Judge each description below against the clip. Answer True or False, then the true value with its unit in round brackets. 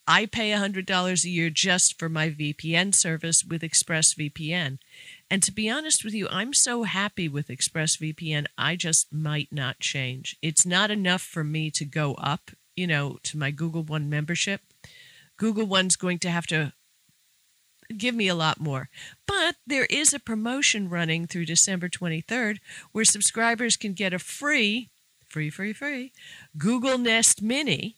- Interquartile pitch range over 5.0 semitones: True (5.6 semitones)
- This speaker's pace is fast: False (160 wpm)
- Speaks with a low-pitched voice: False (180 Hz)